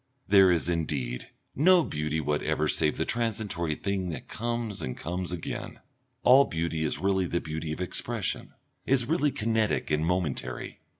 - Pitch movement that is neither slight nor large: No, wide, 6.0 semitones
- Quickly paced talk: No, average, 155 wpm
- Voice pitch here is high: No, very low, 90 Hz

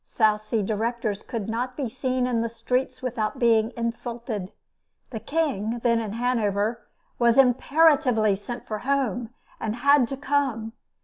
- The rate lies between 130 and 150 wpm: Yes, average, 145 wpm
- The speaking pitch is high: Yes, high, 235 Hz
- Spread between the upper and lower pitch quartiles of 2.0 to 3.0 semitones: Yes, average, 2.7 semitones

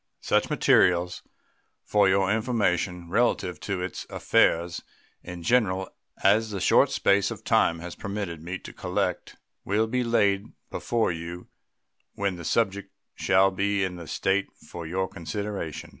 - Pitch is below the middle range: Yes, very low, 95 Hz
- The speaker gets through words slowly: No, average, 145 wpm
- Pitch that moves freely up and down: No, narrow, 2.5 semitones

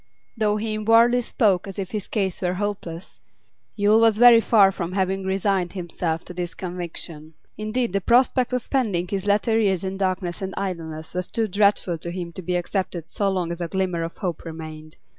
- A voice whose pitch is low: No, high, 190 Hz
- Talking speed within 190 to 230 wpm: Yes, average, 195 wpm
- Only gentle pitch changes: No, average, 3.4 semitones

